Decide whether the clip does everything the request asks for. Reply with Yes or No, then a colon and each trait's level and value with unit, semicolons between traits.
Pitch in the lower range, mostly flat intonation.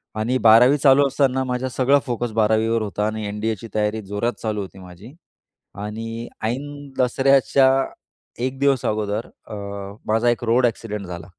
No: low, 115 Hz; average, 3.4 semitones